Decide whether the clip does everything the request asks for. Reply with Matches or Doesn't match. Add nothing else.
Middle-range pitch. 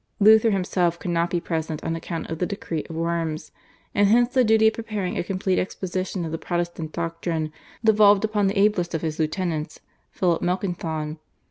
Matches